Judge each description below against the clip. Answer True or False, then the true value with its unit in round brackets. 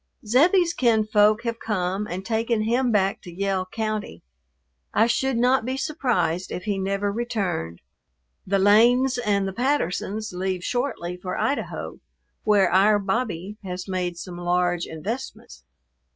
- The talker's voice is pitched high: True (205 Hz)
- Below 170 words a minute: True (135 wpm)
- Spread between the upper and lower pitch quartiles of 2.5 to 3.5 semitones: False (4.2 semitones)